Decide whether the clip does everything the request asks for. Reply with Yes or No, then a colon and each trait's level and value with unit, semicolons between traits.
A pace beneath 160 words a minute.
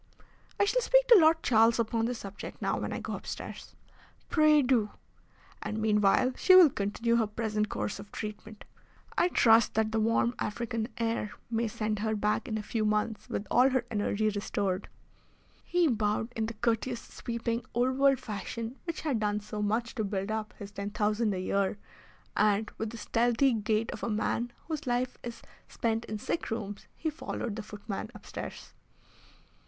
No: average, 180 wpm